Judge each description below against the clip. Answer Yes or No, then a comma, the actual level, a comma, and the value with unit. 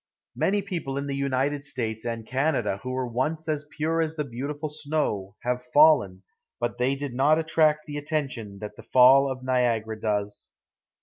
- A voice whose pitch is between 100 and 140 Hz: Yes, low, 135 Hz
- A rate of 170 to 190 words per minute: Yes, average, 175 wpm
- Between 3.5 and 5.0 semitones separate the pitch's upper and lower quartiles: Yes, average, 4.2 semitones